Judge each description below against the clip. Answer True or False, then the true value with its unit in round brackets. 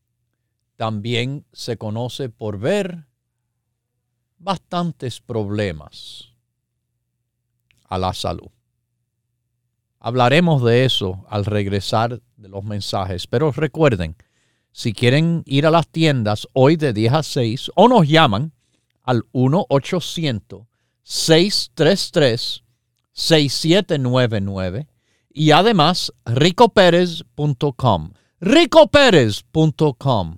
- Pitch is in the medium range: False (120 Hz)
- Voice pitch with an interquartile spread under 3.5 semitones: False (5.2 semitones)